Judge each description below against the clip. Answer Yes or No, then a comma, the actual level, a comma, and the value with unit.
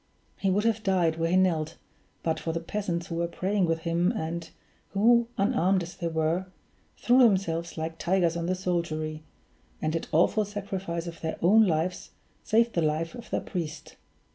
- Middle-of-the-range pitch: Yes, medium, 170 Hz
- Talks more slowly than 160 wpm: No, average, 180 wpm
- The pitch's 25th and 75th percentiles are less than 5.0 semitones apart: Yes, average, 3.1 semitones